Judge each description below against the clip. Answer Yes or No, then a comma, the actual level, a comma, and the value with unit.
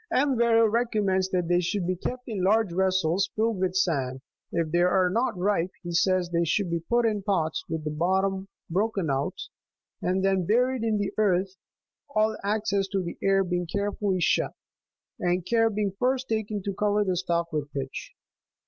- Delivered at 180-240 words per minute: Yes, average, 195 wpm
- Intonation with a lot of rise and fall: No, average, 3.4 semitones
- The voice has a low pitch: No, high, 190 Hz